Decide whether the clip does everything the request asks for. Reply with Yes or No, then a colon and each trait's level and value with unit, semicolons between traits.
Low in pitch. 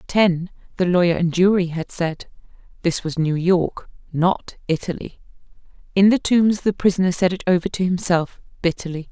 No: medium, 180 Hz